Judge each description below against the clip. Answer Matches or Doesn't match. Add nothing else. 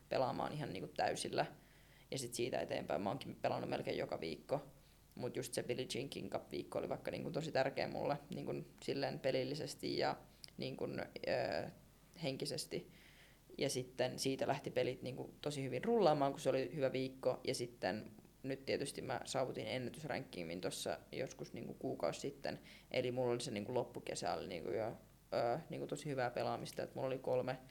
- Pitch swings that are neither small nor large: Doesn't match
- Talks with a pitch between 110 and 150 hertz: Matches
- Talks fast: Matches